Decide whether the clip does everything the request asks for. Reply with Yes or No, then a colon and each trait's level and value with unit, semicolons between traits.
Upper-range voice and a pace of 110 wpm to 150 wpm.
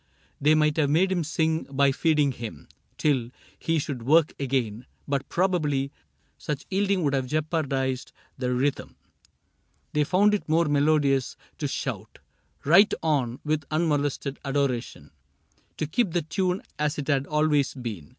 No: medium, 145 Hz; average, 145 wpm